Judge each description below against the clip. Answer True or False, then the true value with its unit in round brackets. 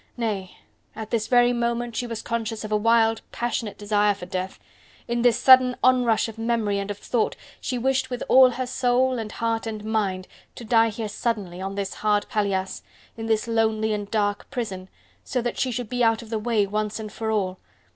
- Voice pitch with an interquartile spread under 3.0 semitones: True (2.4 semitones)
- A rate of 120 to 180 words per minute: False (205 wpm)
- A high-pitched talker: True (225 Hz)